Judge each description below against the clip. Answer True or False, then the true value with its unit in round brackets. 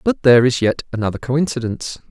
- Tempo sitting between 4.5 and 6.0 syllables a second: False (6.5 syllables/s)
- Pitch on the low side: True (125 Hz)